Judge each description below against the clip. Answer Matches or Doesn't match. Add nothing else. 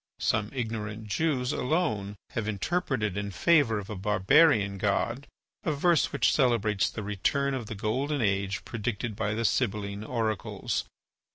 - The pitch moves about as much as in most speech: Matches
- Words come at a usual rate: Matches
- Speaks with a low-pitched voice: Matches